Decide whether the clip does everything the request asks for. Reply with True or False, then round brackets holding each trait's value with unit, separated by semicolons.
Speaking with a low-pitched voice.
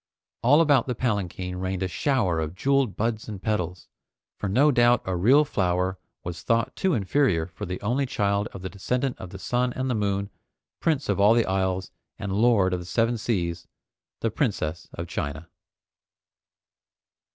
True (100 Hz)